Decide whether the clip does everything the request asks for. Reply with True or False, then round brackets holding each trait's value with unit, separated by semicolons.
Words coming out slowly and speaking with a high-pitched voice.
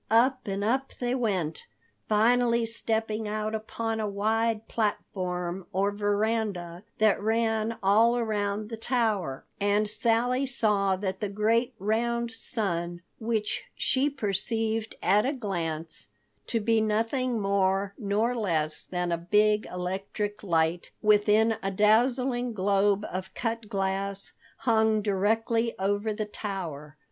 True (120 wpm; 210 Hz)